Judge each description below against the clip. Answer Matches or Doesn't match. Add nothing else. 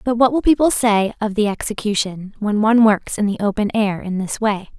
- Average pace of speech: Doesn't match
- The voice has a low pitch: Doesn't match